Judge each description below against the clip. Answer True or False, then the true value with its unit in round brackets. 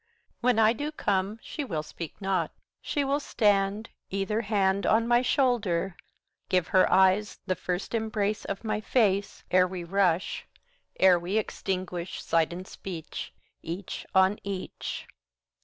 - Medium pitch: False (195 Hz)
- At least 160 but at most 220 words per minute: False (145 wpm)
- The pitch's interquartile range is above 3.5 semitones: False (2.9 semitones)